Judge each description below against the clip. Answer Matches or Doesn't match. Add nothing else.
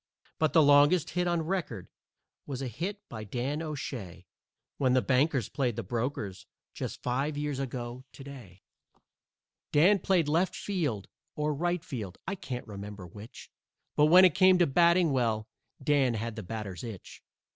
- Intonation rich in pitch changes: Matches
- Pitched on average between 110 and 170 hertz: Matches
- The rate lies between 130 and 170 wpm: Matches